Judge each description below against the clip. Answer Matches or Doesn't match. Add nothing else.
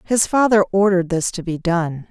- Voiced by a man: Doesn't match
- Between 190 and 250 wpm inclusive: Matches